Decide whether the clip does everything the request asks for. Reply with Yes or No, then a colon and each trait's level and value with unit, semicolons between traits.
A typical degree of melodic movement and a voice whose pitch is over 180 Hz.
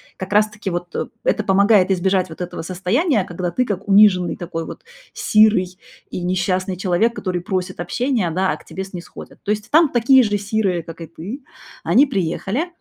Yes: average, 3.2 semitones; high, 190 Hz